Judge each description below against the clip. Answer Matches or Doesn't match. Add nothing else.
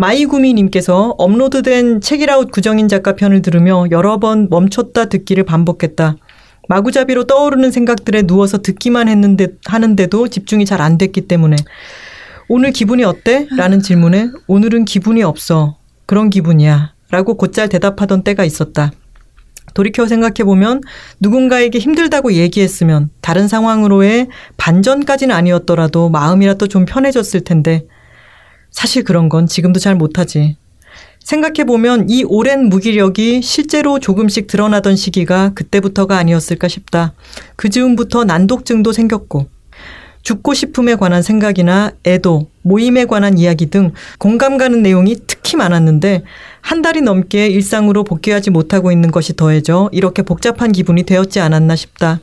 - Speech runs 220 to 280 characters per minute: Doesn't match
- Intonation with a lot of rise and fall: Doesn't match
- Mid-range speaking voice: Doesn't match